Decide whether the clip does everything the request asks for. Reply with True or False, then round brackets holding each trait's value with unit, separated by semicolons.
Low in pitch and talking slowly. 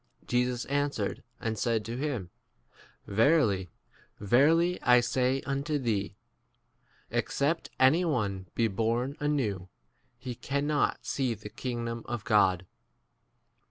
True (120 Hz; 120 wpm)